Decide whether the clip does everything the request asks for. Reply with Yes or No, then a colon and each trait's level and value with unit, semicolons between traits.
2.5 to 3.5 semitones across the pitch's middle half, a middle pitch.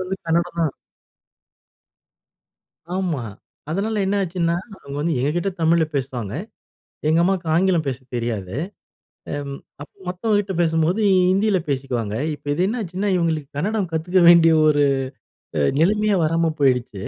No: average, 4.5 semitones; medium, 165 Hz